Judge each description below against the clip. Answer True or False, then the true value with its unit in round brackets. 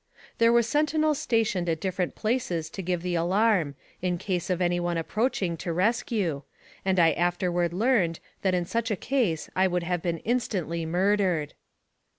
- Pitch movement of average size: True (4.1 semitones)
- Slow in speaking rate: False (165 wpm)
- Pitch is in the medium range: True (180 Hz)